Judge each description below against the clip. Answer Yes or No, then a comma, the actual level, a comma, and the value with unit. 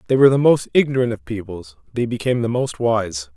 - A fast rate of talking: Yes, fast, 215 wpm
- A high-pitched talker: No, low, 120 Hz